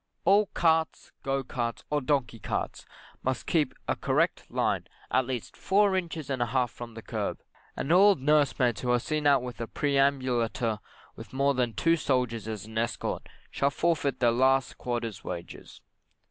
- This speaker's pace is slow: No, average, 170 wpm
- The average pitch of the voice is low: Yes, low, 130 Hz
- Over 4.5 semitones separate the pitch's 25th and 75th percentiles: No, average, 3.8 semitones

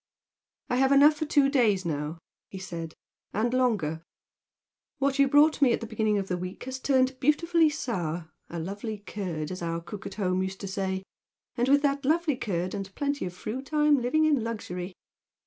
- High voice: Yes, high, 220 Hz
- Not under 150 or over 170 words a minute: No, average, 190 wpm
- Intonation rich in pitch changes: Yes, wide, 7.1 semitones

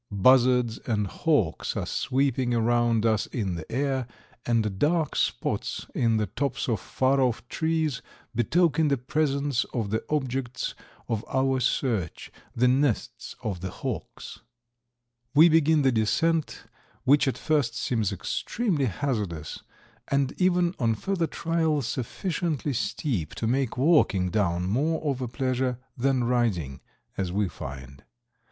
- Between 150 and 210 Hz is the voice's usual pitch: No, low, 125 Hz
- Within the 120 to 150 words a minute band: Yes, slow, 135 wpm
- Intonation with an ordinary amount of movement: Yes, average, 4.6 semitones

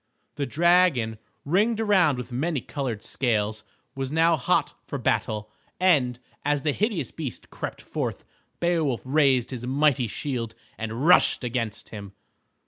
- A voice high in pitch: No, low, 135 Hz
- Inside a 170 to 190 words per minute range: No, slow, 135 wpm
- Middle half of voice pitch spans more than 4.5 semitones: Yes, wide, 5.5 semitones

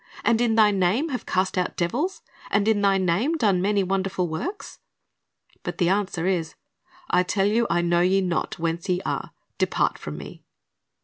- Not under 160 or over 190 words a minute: Yes, average, 180 wpm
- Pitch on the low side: No, high, 195 Hz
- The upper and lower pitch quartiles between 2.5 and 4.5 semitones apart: Yes, average, 3.4 semitones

